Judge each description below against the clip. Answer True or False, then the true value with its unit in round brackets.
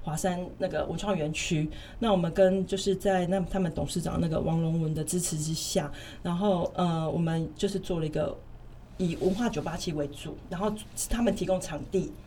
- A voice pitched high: False (180 Hz)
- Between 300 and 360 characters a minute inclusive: False (285 characters per minute)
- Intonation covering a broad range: False (3.6 semitones)